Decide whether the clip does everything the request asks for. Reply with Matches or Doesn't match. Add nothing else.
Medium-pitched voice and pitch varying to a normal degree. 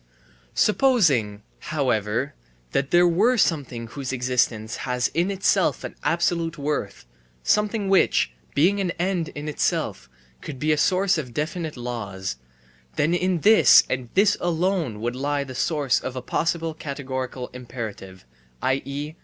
Doesn't match